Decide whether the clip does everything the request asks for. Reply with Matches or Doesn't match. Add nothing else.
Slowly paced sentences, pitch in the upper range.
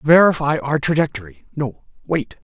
Doesn't match